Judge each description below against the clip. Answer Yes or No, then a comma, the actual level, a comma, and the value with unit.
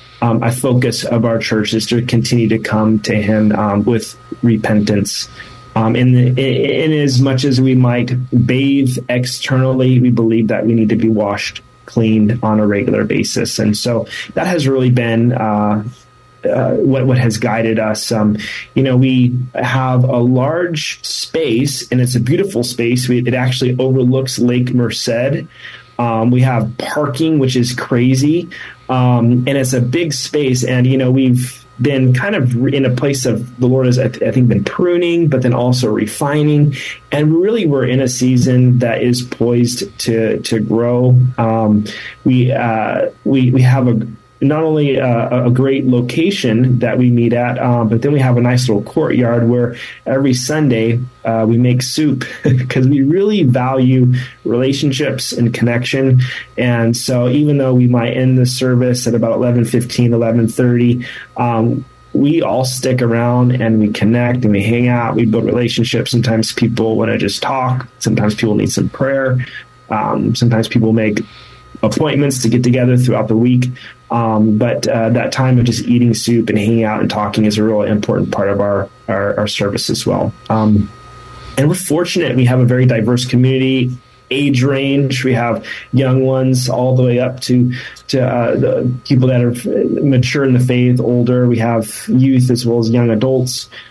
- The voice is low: Yes, low, 125 Hz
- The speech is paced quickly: No, average, 175 wpm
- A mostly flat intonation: Yes, narrow, 2.0 semitones